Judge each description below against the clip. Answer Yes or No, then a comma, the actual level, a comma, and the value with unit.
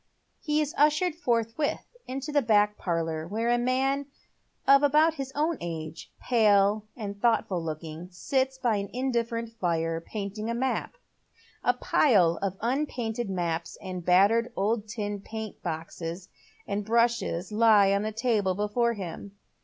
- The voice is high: Yes, high, 220 Hz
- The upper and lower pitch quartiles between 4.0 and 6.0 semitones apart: Yes, average, 4.5 semitones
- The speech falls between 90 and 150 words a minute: Yes, average, 145 wpm